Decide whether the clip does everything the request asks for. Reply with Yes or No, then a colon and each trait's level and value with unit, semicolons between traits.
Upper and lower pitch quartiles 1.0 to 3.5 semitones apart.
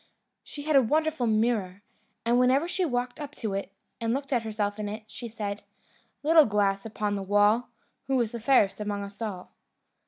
No: average, 4.0 semitones